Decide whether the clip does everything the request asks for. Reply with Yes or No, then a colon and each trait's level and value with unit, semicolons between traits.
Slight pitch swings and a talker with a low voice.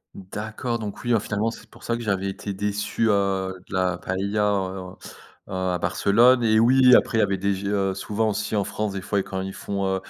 Yes: narrow, 2.3 semitones; low, 100 Hz